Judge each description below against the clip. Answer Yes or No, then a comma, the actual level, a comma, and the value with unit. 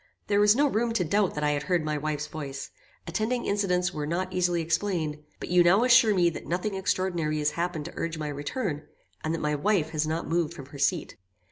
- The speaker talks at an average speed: No, fast, 225 wpm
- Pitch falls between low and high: Yes, medium, 170 Hz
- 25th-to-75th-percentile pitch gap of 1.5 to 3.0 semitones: No, average, 3.9 semitones